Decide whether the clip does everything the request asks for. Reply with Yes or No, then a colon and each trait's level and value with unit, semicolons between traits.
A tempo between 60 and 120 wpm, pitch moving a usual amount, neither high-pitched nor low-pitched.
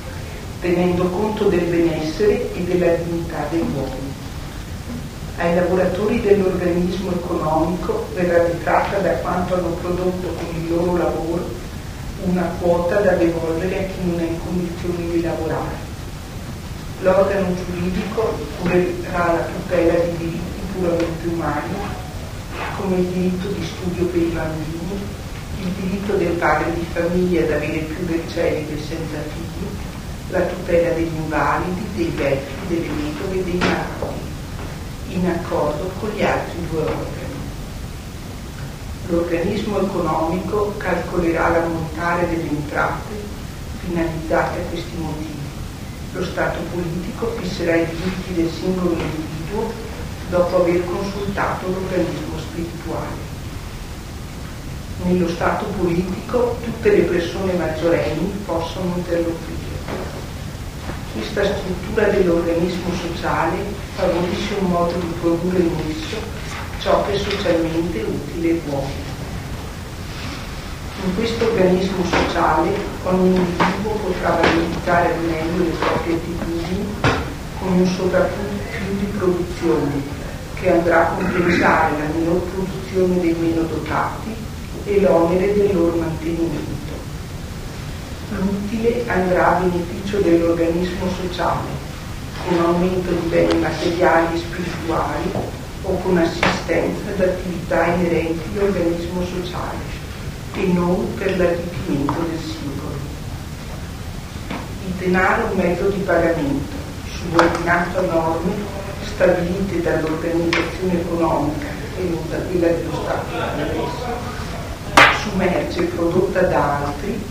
No: slow, 115 wpm; narrow, 1.9 semitones; medium, 175 Hz